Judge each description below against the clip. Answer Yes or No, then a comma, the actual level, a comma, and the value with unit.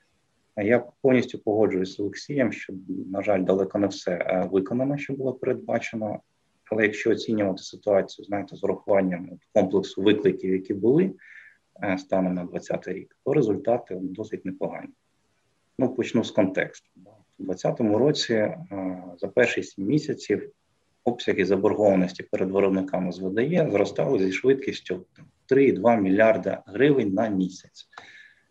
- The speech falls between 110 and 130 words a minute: Yes, average, 125 wpm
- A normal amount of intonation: No, narrow, 2.3 semitones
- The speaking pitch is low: Yes, very low, 95 Hz